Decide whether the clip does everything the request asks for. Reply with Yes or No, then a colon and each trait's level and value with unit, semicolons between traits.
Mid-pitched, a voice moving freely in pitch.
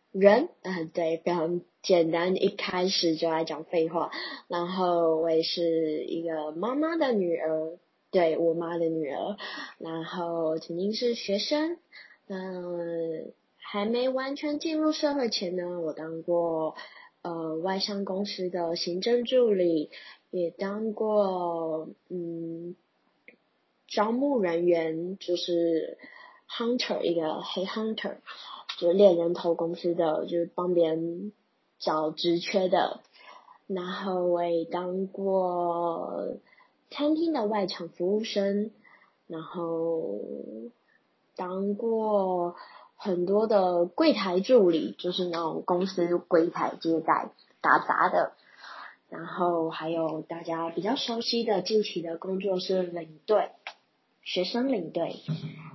No: medium, 175 Hz; average, 3.4 semitones